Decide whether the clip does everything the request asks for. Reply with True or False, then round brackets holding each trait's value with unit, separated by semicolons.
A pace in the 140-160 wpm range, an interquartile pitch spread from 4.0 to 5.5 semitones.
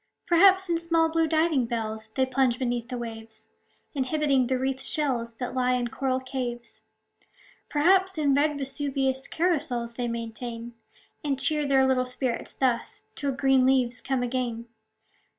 False (150 wpm; 3.4 semitones)